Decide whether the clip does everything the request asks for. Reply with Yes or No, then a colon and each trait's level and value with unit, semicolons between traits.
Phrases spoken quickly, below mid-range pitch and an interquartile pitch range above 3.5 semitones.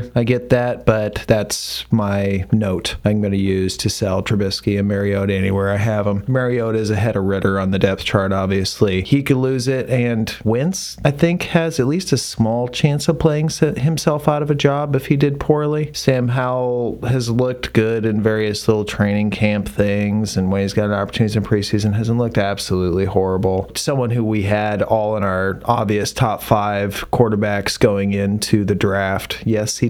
No: average, 190 wpm; low, 110 Hz; average, 4.0 semitones